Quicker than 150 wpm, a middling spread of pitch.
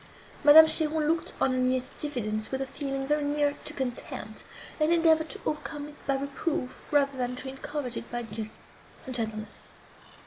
Yes: average, 165 wpm; average, 3.0 semitones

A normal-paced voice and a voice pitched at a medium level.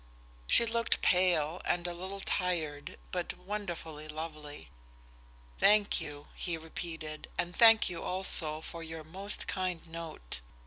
No: slow, 130 wpm; medium, 170 Hz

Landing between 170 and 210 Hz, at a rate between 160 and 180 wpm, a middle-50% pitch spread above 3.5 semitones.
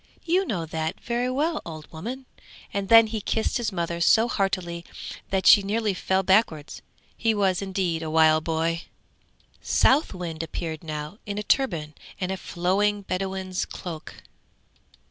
No: high, 190 Hz; average, 150 wpm; average, 4.6 semitones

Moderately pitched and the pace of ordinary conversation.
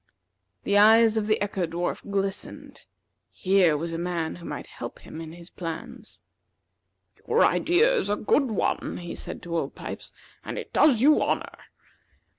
No: high, 195 Hz; average, 165 wpm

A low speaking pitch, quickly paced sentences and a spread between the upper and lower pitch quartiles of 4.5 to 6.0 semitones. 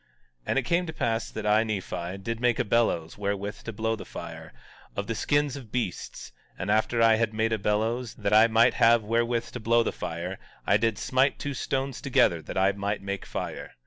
No: low, 110 Hz; fast, 215 wpm; narrow, 2.6 semitones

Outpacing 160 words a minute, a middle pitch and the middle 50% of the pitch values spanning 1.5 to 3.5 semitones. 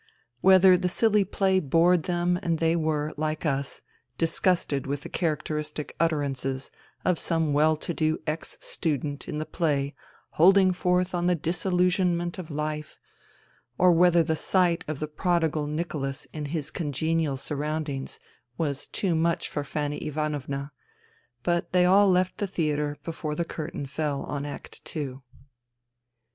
No: average, 150 wpm; medium, 160 Hz; average, 3.0 semitones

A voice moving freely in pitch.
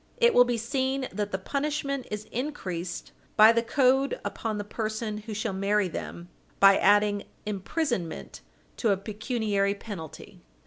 No: average, 4.1 semitones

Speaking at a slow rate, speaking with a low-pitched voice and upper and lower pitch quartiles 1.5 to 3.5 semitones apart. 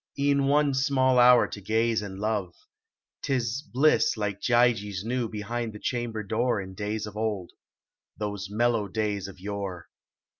No: average, 155 wpm; low, 110 Hz; average, 3.2 semitones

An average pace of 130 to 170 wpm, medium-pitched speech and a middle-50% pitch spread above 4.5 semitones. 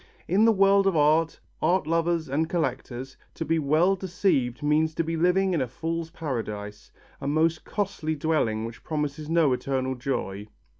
No: average, 165 wpm; medium, 155 Hz; average, 4.1 semitones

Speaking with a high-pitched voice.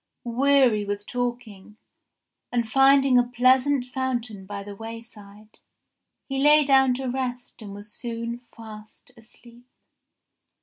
Yes: high, 240 Hz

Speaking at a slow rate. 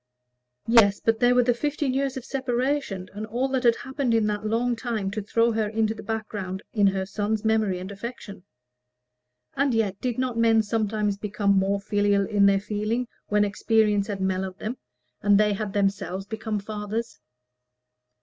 No: average, 175 wpm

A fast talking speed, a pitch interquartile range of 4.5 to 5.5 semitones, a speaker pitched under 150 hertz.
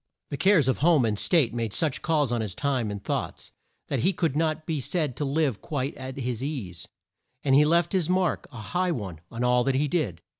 Yes: fast, 225 wpm; average, 5.0 semitones; medium, 140 Hz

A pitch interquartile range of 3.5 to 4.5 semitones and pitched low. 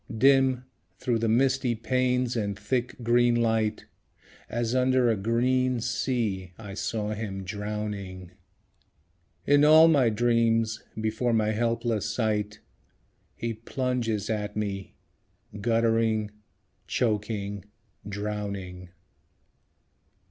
No: average, 2.7 semitones; low, 115 Hz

